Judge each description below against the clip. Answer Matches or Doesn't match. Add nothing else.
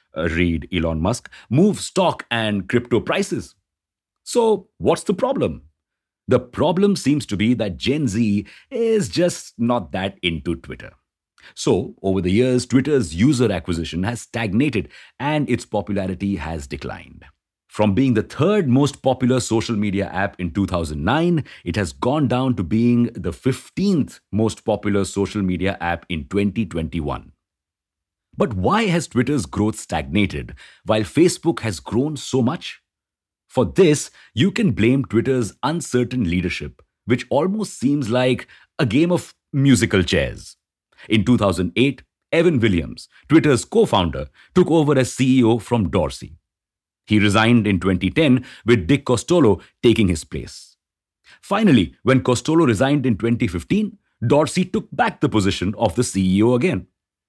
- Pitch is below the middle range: Matches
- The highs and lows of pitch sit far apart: Matches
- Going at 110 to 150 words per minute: Matches